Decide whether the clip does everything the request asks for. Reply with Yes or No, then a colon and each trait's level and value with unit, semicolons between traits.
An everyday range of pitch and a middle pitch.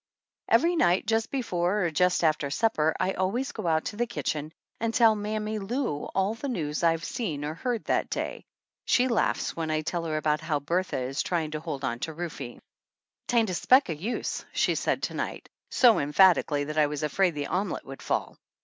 No: wide, 6.2 semitones; medium, 175 Hz